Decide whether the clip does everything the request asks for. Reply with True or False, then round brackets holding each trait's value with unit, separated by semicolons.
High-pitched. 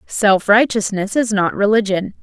True (205 Hz)